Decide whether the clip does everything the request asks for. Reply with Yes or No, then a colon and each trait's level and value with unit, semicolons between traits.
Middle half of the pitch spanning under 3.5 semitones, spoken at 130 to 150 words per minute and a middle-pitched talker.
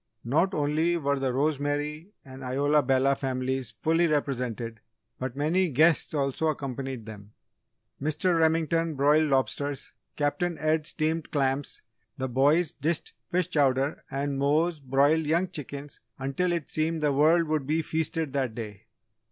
Yes: average, 3.1 semitones; average, 140 wpm; medium, 145 Hz